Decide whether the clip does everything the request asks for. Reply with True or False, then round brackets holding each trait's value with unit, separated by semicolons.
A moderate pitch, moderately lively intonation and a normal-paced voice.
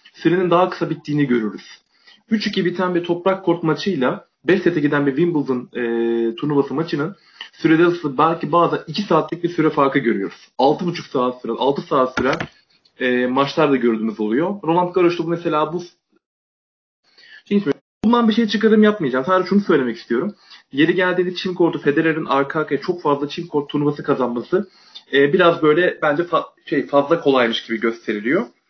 False (160 Hz; 4.5 semitones; 160 wpm)